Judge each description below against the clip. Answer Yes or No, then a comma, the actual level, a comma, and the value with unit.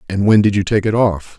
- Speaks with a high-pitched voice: No, low, 100 Hz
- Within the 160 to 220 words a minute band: No, fast, 305 wpm